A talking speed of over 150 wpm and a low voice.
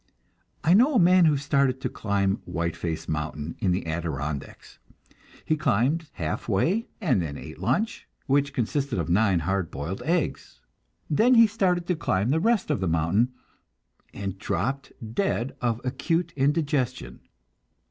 No: average, 145 wpm; low, 130 Hz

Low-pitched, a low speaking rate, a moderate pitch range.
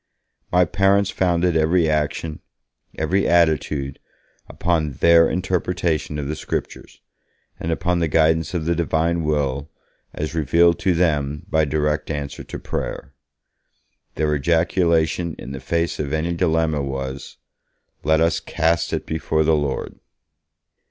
No: very low, 80 Hz; slow, 130 wpm; narrow, 2.1 semitones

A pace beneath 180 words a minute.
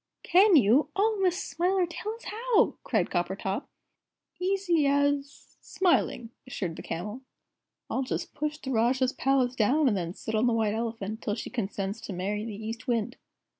Yes: average, 170 wpm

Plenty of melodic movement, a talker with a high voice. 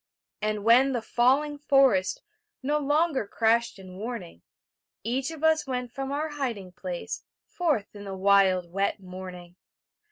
Yes: wide, 6.2 semitones; high, 230 Hz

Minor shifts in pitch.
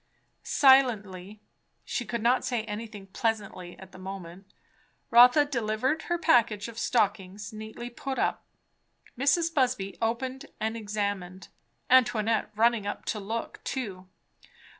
No: average, 3.5 semitones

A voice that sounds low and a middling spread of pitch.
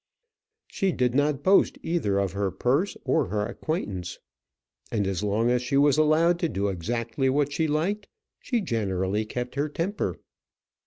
No: low, 125 Hz; wide, 7.2 semitones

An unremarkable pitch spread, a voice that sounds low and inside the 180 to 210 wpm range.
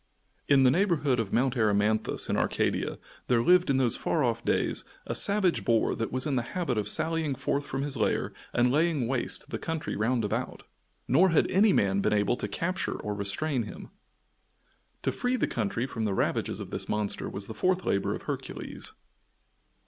No: wide, 6.7 semitones; low, 130 Hz; average, 190 wpm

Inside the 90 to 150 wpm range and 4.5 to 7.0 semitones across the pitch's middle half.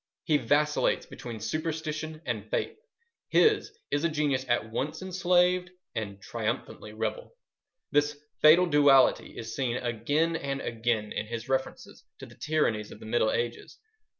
Yes: average, 145 wpm; average, 5.3 semitones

